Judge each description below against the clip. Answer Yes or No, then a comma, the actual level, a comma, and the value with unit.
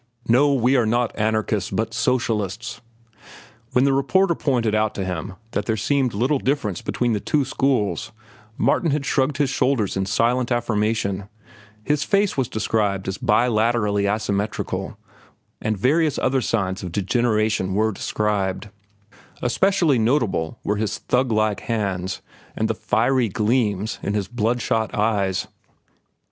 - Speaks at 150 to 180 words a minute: No, average, 140 wpm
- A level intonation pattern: No, average, 3.9 semitones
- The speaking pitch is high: No, low, 110 Hz